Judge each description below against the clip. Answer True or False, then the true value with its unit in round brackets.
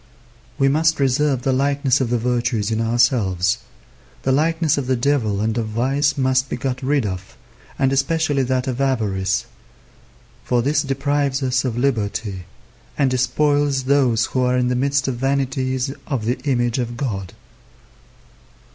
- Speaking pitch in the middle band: False (130 Hz)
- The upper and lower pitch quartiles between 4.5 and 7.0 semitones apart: False (2.7 semitones)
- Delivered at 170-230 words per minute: False (155 wpm)